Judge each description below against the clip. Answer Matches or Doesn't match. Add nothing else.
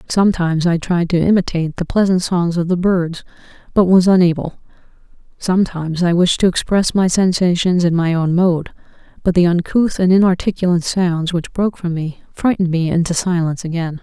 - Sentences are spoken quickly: Doesn't match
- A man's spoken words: Doesn't match